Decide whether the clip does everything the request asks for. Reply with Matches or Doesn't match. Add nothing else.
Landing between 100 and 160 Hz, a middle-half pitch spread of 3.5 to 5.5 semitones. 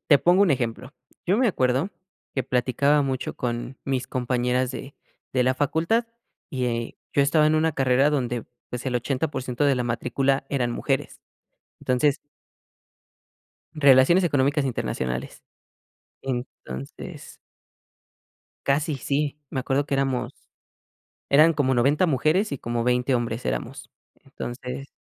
Doesn't match